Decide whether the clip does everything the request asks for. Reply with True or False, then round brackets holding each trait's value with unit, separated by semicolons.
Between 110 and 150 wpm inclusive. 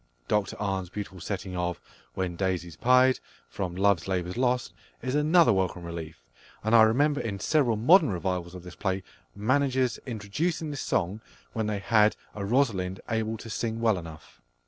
False (165 wpm)